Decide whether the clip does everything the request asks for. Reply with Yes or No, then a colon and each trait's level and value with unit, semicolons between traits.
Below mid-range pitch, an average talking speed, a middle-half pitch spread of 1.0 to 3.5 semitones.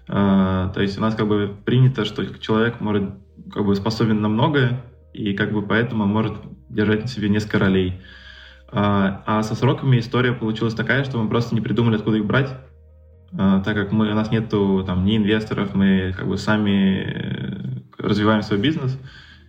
No: low, 105 Hz; fast, 175 wpm; narrow, 2.5 semitones